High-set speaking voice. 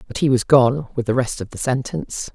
No: low, 130 Hz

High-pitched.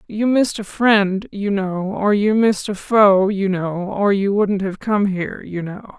Yes: high, 200 Hz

